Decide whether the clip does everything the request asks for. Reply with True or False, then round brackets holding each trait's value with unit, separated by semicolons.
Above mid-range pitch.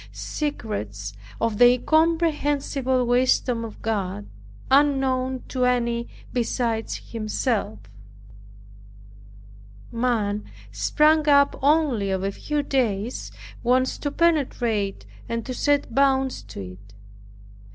True (250 Hz)